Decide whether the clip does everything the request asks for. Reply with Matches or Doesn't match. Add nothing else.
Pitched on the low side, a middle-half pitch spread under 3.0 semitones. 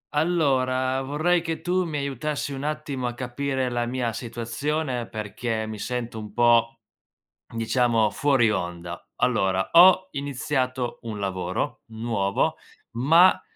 Doesn't match